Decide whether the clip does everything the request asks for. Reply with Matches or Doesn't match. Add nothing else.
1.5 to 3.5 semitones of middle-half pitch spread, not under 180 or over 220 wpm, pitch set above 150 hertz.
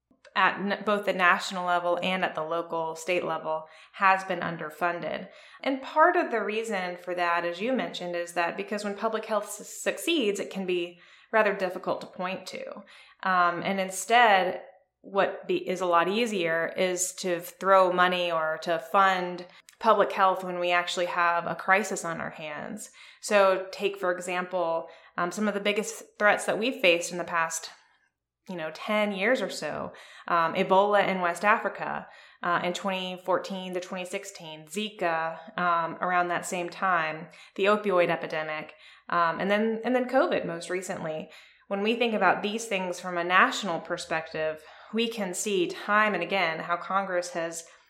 Doesn't match